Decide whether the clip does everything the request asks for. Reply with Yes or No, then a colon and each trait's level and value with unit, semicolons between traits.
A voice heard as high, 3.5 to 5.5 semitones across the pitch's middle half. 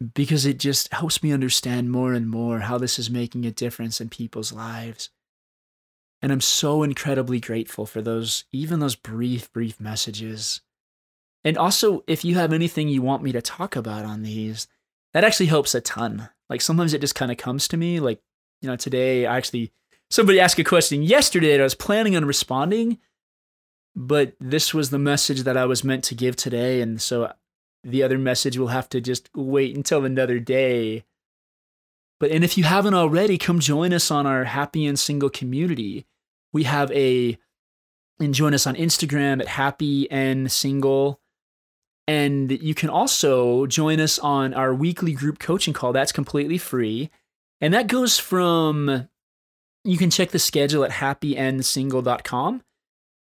No: low, 135 Hz; average, 4.0 semitones